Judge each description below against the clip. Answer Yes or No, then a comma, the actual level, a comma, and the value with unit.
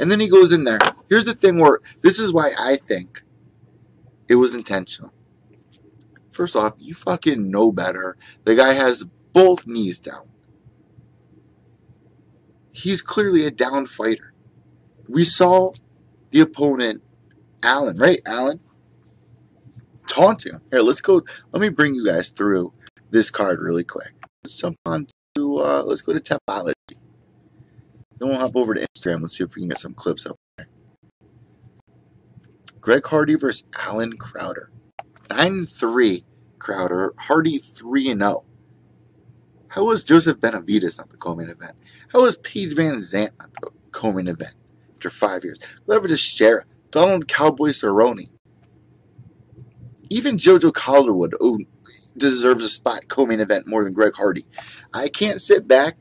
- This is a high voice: No, low, 135 Hz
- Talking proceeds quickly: No, average, 145 wpm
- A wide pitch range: Yes, wide, 8.7 semitones